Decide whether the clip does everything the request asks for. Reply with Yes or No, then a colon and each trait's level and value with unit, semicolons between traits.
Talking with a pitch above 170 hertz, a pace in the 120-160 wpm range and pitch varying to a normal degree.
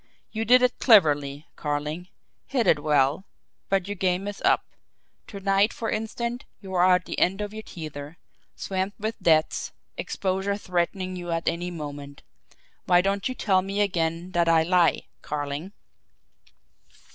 Yes: medium, 185 Hz; average, 155 wpm; average, 3.9 semitones